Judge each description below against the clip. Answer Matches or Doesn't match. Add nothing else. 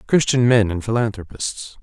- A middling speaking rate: Doesn't match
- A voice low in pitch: Matches